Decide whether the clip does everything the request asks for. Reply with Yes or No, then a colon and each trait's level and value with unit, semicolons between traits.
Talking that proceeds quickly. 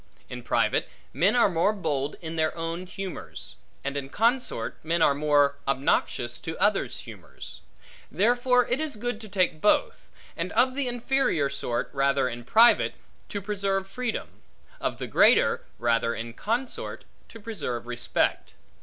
No: average, 150 wpm